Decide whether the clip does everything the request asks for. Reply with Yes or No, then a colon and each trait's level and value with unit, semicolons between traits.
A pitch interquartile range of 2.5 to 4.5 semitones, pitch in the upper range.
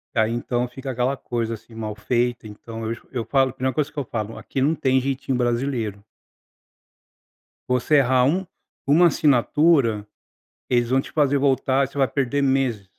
No: average, 2.8 semitones; low, 130 Hz